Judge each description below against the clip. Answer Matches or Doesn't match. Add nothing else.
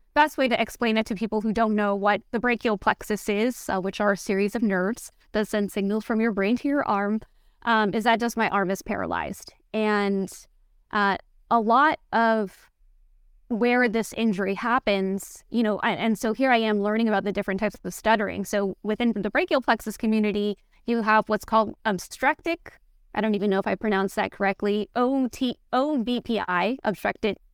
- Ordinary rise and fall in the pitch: Doesn't match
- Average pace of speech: Matches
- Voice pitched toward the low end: Doesn't match